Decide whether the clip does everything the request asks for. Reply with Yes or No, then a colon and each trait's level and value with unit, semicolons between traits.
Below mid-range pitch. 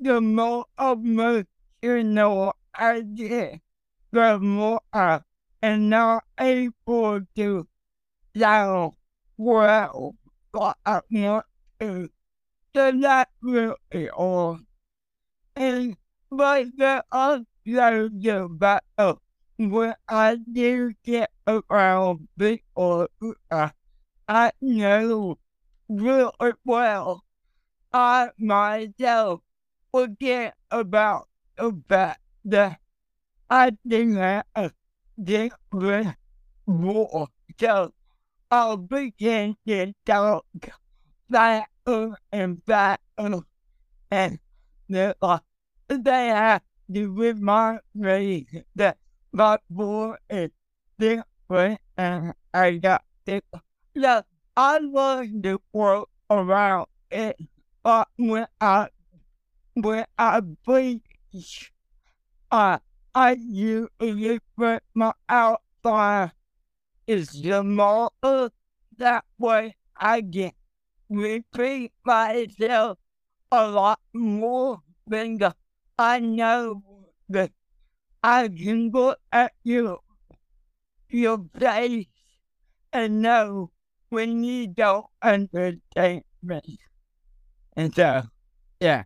No: high, 215 Hz